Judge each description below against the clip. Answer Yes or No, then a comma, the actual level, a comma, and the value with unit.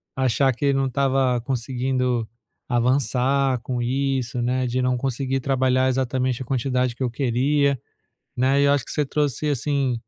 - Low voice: Yes, low, 130 Hz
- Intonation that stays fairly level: Yes, narrow, 1.6 semitones